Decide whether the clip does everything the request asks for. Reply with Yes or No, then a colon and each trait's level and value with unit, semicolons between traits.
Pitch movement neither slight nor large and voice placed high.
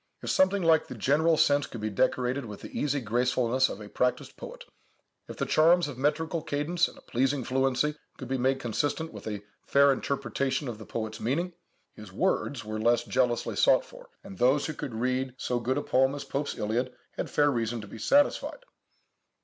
No: average, 3.7 semitones; low, 130 Hz